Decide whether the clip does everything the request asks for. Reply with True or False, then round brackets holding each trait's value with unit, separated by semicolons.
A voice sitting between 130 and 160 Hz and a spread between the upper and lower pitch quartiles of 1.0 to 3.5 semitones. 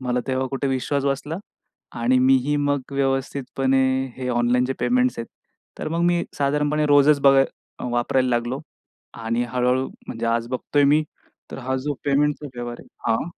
True (135 Hz; 2.4 semitones)